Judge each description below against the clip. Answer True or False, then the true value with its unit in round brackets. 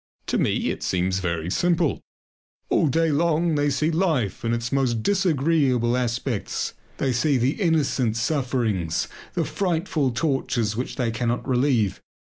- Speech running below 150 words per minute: True (140 wpm)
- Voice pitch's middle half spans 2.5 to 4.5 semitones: False (5.2 semitones)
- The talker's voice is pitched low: True (130 Hz)